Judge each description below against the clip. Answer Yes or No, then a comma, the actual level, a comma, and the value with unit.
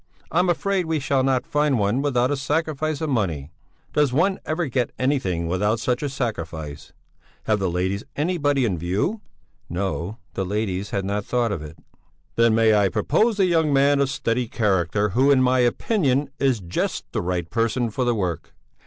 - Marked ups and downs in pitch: Yes, wide, 6.5 semitones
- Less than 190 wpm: Yes, average, 180 wpm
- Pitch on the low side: Yes, low, 120 Hz